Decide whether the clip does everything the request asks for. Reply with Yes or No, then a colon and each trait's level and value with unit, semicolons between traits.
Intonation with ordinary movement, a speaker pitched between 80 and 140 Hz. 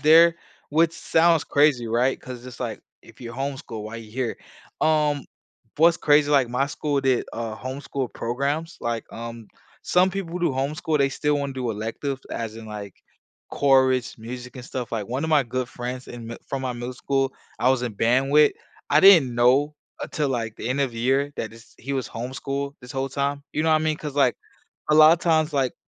Yes: average, 3.5 semitones; low, 135 Hz